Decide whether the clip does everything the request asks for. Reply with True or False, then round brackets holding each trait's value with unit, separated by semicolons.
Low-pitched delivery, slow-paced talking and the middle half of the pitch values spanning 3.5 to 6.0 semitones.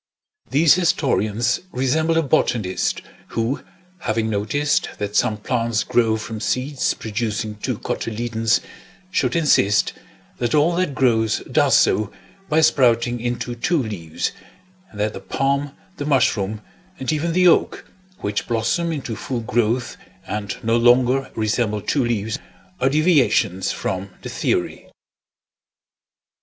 True (120 Hz; 125 wpm; 4.4 semitones)